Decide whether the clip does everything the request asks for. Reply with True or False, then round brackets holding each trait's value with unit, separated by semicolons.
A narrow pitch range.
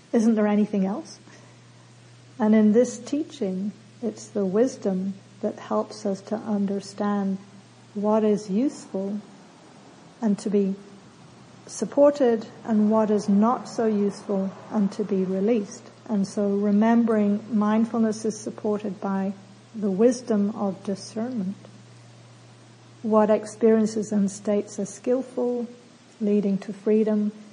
True (1.8 semitones)